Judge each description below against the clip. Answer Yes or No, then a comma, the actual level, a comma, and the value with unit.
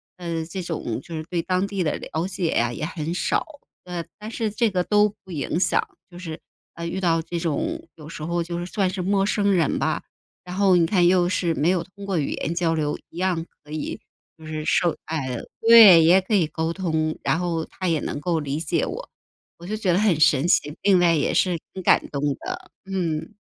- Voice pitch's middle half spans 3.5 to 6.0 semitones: No, average, 2.8 semitones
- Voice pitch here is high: No, medium, 175 Hz